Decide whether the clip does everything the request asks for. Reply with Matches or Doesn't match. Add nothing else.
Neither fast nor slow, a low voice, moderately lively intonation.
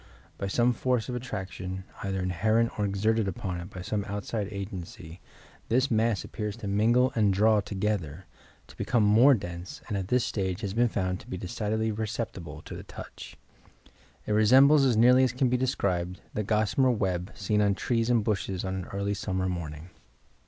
Matches